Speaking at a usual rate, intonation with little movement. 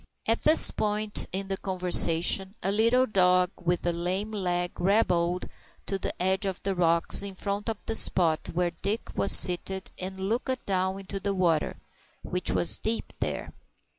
Yes: average, 165 wpm; narrow, 2.3 semitones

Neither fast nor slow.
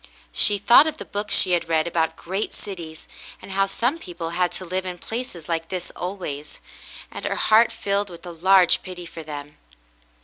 Yes: average, 195 wpm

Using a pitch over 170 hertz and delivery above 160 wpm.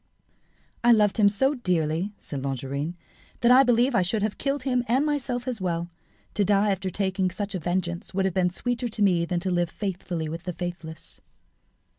Yes: high, 190 Hz; average, 195 wpm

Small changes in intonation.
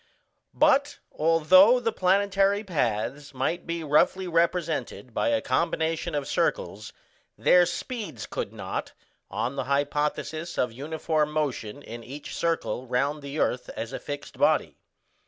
No: average, 4.4 semitones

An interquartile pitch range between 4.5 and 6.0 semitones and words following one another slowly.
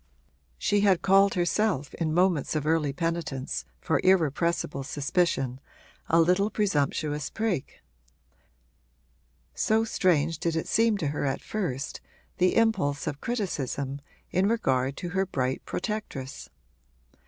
Yes: wide, 5.5 semitones; slow, 120 wpm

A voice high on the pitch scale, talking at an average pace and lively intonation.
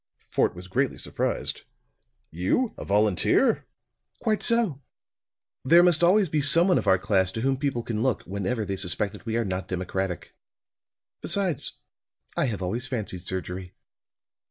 No: low, 110 Hz; average, 155 wpm; wide, 7.4 semitones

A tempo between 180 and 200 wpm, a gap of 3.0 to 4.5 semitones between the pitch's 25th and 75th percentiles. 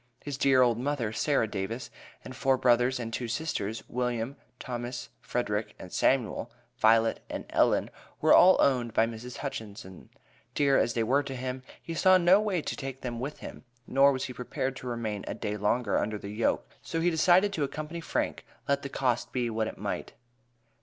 Yes: average, 190 wpm; average, 3.6 semitones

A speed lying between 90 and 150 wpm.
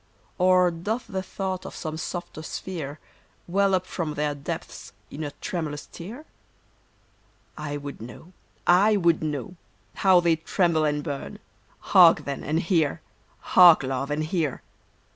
Yes: average, 145 wpm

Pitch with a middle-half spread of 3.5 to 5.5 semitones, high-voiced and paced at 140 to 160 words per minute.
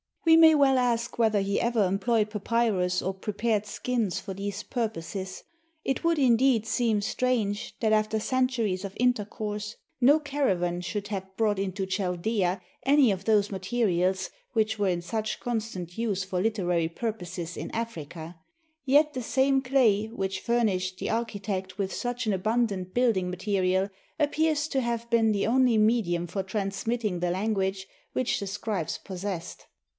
Yes: average, 3.8 semitones; high, 210 Hz; average, 155 wpm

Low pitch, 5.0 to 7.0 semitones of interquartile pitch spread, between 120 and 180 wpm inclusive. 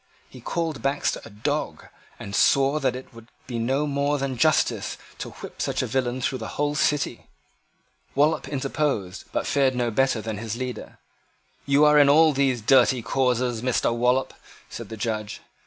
No: low, 130 Hz; average, 3.3 semitones; average, 170 wpm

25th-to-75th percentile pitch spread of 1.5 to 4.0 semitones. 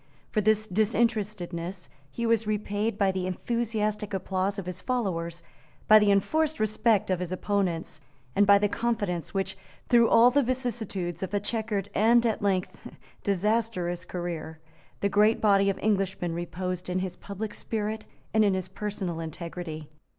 Yes: average, 3.1 semitones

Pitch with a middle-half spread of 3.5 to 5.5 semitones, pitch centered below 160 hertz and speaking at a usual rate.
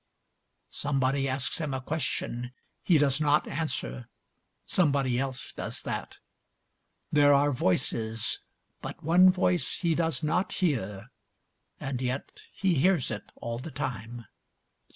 No: average, 4.3 semitones; medium, 140 Hz; slow, 125 wpm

